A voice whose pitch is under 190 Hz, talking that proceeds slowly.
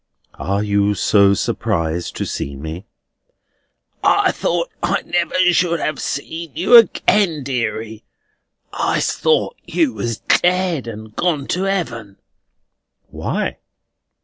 Yes: low, 135 Hz; slow, 115 wpm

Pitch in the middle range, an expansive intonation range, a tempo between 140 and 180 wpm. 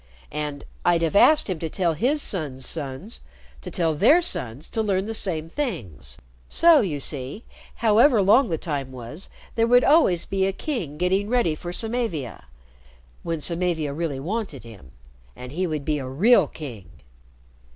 Yes: medium, 170 Hz; wide, 7.1 semitones; average, 165 wpm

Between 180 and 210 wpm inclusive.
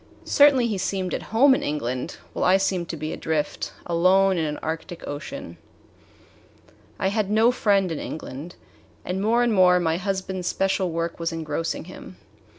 No: average, 165 wpm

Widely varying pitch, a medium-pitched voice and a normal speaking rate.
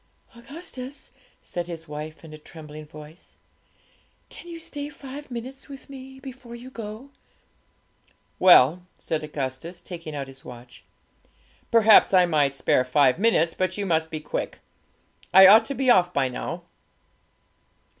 Yes: wide, 8.7 semitones; medium, 180 Hz; average, 145 wpm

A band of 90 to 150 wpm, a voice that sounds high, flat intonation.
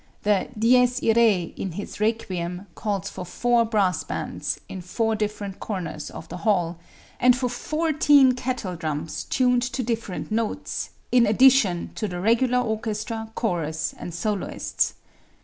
No: slow, 135 wpm; high, 215 Hz; average, 5.1 semitones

